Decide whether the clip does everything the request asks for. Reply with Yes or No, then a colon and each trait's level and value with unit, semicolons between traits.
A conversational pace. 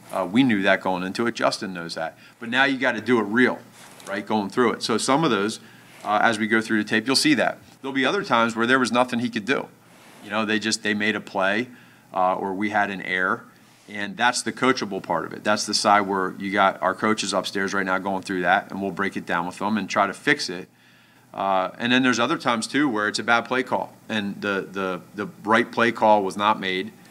No: fast, 260 wpm